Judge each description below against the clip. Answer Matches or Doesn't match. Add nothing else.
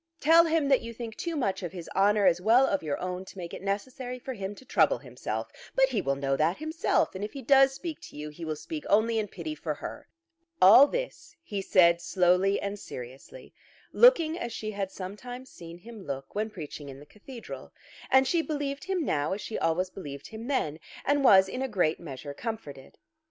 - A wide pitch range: Matches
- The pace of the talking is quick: Matches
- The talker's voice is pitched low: Doesn't match